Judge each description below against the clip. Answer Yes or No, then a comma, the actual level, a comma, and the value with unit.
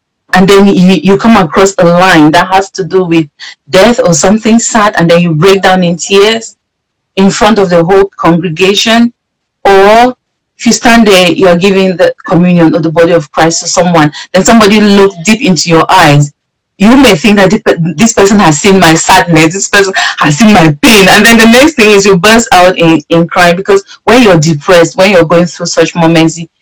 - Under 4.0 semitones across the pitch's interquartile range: Yes, average, 3.4 semitones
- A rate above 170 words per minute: Yes, fast, 205 wpm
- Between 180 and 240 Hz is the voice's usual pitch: Yes, high, 190 Hz